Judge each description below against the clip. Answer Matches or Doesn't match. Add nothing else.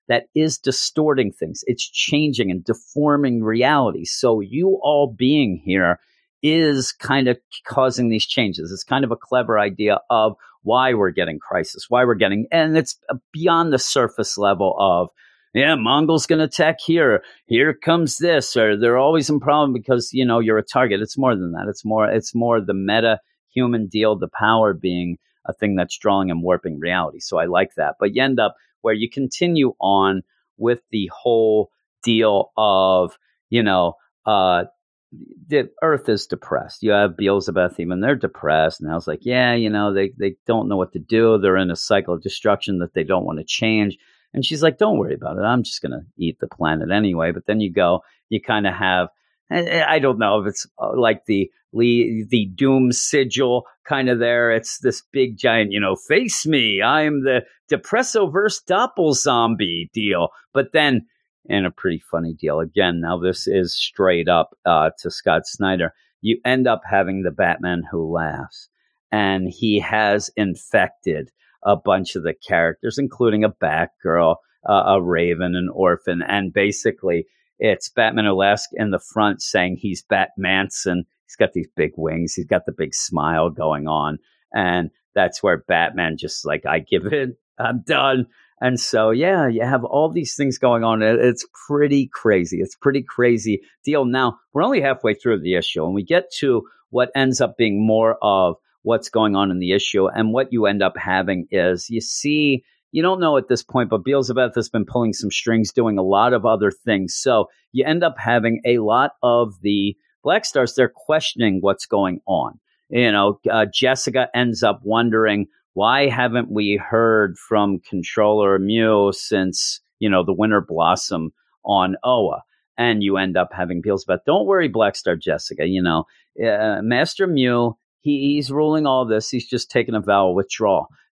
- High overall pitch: Doesn't match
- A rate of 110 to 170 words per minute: Doesn't match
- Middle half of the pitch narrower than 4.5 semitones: Doesn't match